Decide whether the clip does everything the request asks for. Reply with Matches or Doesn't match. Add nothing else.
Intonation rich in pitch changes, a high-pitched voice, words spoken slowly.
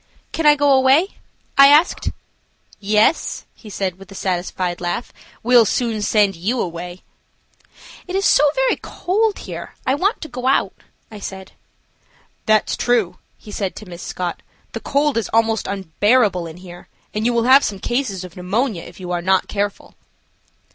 Doesn't match